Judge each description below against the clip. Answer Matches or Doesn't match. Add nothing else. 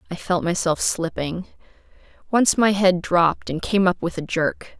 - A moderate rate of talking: Matches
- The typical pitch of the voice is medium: Matches